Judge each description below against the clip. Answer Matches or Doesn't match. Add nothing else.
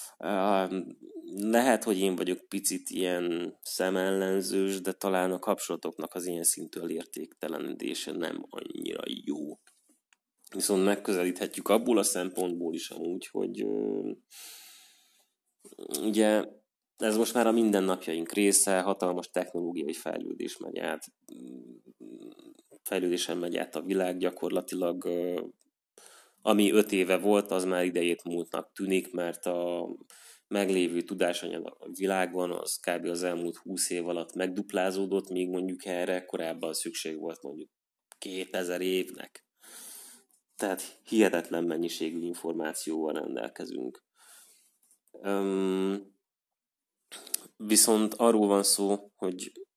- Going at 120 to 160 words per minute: Doesn't match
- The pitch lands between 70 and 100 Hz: Matches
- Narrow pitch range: Matches